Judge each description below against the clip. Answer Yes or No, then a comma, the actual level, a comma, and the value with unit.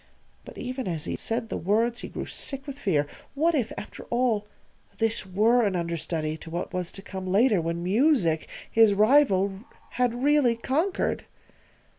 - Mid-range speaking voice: No, high, 220 Hz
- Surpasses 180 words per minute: No, average, 165 wpm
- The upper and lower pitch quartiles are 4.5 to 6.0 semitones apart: Yes, wide, 5.5 semitones